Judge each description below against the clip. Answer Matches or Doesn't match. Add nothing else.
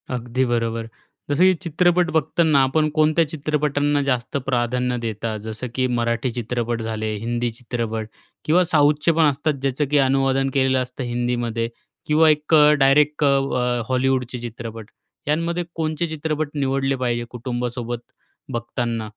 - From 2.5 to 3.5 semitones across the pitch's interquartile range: Doesn't match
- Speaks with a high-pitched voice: Doesn't match